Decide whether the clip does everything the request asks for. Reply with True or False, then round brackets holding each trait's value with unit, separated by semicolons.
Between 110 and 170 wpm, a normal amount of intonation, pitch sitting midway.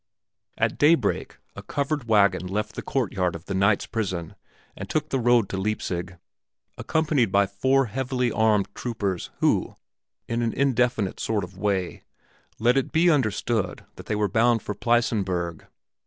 False (155 wpm; 4.1 semitones; 110 Hz)